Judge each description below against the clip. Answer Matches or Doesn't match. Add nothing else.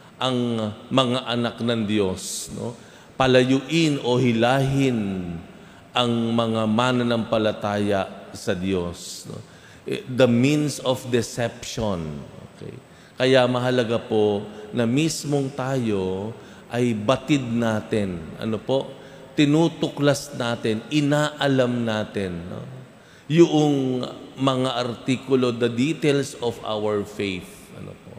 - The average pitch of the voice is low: Matches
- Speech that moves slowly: Matches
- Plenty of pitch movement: Doesn't match